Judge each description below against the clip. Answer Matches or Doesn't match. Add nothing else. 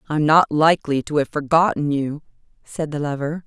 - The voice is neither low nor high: Matches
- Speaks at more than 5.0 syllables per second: Matches